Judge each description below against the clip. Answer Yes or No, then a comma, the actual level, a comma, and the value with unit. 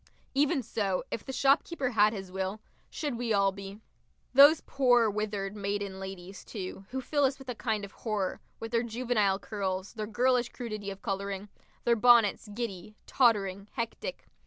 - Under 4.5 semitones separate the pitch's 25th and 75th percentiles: Yes, average, 3.7 semitones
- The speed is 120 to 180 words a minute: Yes, average, 165 wpm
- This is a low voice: No, high, 215 Hz